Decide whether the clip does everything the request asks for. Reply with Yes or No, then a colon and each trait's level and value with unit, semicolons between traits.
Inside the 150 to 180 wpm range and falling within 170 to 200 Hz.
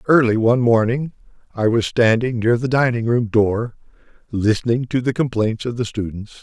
No: average, 170 wpm; low, 115 Hz